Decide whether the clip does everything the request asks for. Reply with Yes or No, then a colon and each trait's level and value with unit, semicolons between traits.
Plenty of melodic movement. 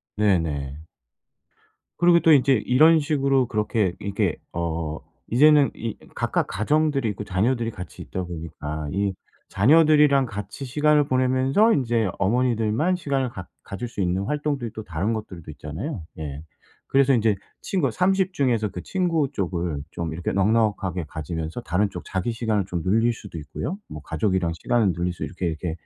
Yes: wide, 7.4 semitones